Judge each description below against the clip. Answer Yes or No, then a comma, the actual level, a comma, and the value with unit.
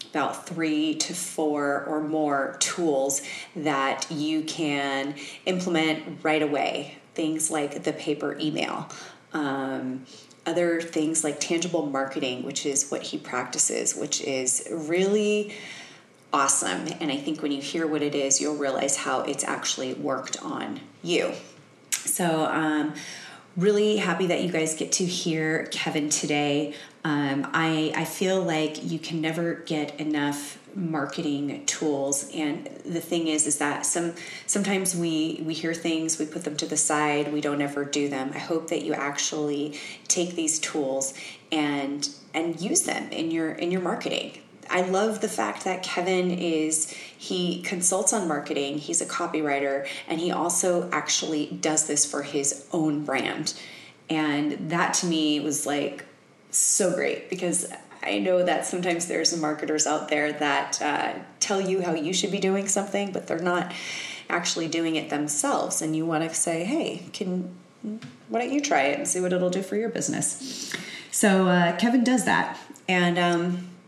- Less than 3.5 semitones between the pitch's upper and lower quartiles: Yes, average, 3.1 semitones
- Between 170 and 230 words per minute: No, average, 160 wpm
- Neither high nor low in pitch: Yes, medium, 155 Hz